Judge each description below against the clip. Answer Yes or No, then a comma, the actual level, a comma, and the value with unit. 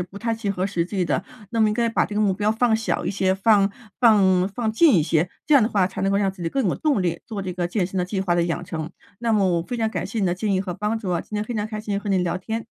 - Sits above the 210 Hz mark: No, high, 200 Hz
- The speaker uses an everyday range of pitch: Yes, average, 3.3 semitones